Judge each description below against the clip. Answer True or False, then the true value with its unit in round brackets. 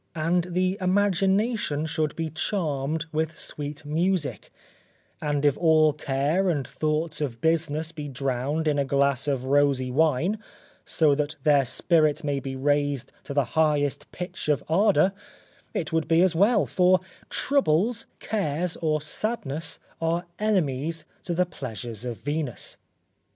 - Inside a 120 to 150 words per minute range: True (140 wpm)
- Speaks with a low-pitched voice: False (155 Hz)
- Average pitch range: True (3.5 semitones)